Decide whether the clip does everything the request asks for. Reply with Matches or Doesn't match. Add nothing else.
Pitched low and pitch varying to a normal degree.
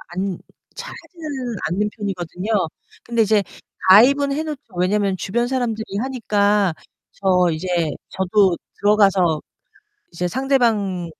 Doesn't match